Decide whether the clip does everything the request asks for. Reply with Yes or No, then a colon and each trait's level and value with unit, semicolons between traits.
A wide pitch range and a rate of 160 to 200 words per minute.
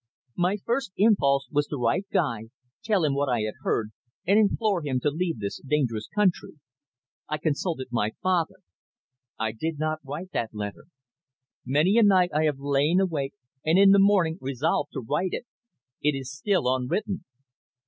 Yes: wide, 5.7 semitones; average, 170 wpm